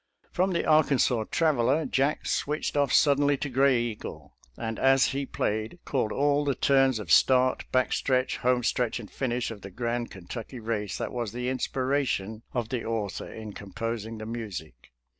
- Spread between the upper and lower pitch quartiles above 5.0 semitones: No, average, 3.5 semitones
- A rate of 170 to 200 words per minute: Yes, average, 180 wpm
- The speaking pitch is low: Yes, low, 125 Hz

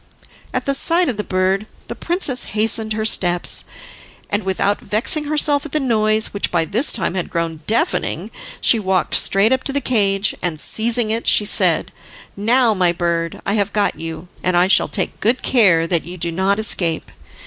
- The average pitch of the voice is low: No, high, 205 Hz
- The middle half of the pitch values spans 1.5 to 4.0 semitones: No, average, 4.4 semitones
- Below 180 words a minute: No, average, 190 wpm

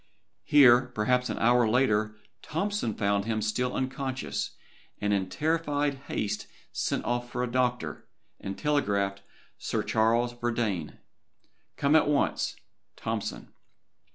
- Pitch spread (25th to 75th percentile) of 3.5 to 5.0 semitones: Yes, average, 3.8 semitones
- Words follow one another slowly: Yes, slow, 125 wpm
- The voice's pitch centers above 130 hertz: No, low, 120 Hz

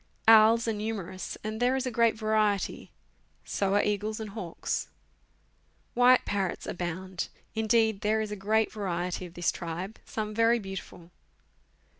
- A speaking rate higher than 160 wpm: No, average, 145 wpm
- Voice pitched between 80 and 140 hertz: No, high, 210 Hz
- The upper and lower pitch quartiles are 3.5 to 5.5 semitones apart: No, average, 2.7 semitones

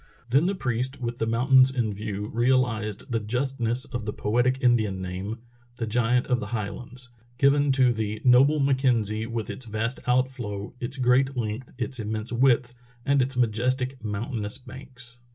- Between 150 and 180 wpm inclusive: Yes, average, 160 wpm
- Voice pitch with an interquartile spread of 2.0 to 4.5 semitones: Yes, average, 3.0 semitones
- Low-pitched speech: Yes, low, 120 Hz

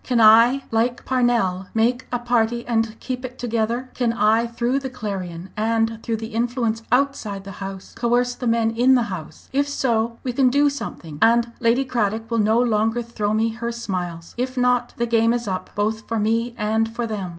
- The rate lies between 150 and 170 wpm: No, average, 195 wpm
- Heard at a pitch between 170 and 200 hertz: No, high, 230 Hz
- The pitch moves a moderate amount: No, narrow, 1.9 semitones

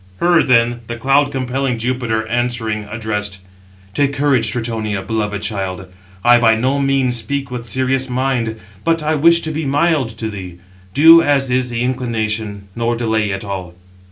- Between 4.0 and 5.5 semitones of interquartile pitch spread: No, average, 3.6 semitones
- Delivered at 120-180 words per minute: Yes, average, 160 wpm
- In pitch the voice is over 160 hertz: No, low, 120 Hz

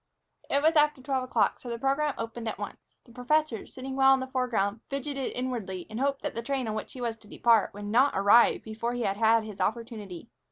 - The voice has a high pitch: Yes, high, 240 Hz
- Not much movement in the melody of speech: No, average, 3.4 semitones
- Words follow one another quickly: Yes, fast, 230 wpm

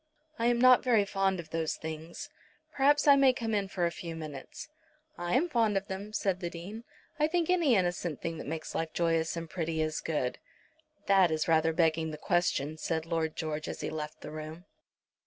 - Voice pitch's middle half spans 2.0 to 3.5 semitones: No, average, 5.0 semitones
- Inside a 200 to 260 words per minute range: Yes, fast, 205 wpm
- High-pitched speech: No, medium, 170 Hz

